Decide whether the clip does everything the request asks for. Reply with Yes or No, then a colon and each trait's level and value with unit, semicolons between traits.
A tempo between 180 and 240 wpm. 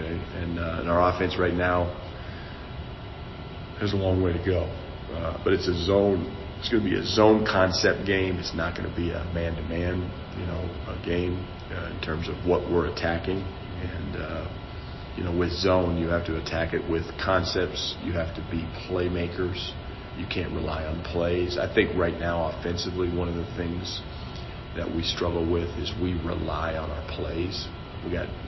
Yes: average, 185 wpm